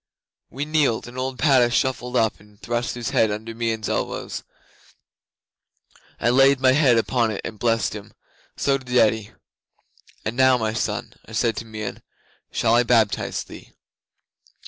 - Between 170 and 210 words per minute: No, average, 155 wpm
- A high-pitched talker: No, low, 120 Hz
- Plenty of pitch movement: No, narrow, 2.6 semitones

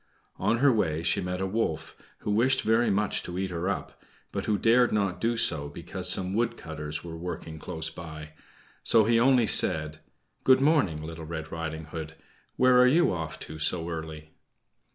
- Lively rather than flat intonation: Yes, wide, 6.0 semitones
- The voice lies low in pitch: Yes, very low, 90 Hz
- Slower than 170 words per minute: No, average, 185 wpm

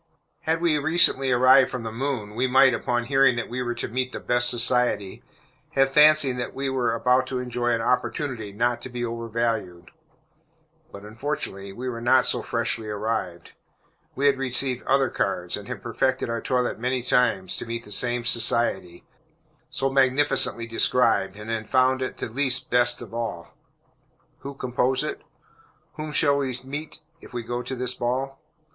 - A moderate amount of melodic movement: No, narrow, 2.3 semitones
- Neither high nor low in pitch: No, low, 125 Hz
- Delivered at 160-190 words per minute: Yes, average, 175 wpm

